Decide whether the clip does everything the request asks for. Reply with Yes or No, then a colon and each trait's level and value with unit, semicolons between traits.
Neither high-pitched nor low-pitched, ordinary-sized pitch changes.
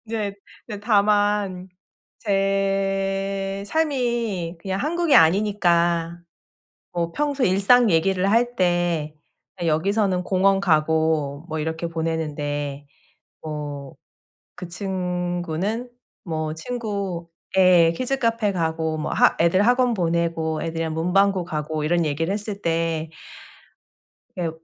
Yes: medium, 180 Hz; average, 3.7 semitones